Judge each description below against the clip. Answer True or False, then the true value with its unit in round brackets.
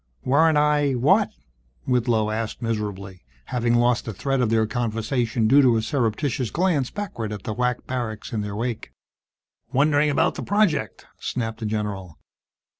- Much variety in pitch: False (3.9 semitones)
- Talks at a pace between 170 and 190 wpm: False (155 wpm)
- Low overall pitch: True (120 Hz)